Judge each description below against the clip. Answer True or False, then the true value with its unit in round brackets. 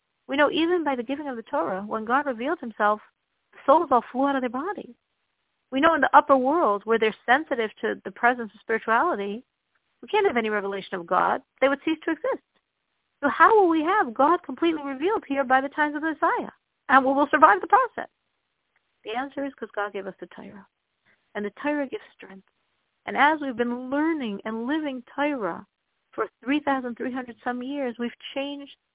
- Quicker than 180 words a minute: True (205 wpm)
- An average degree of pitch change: True (4.7 semitones)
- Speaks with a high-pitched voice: True (270 Hz)